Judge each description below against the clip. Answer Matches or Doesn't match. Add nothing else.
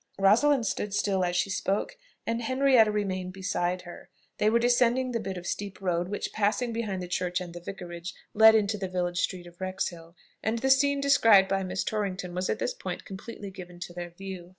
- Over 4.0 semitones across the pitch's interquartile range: Doesn't match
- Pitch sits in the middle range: Doesn't match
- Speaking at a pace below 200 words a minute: Doesn't match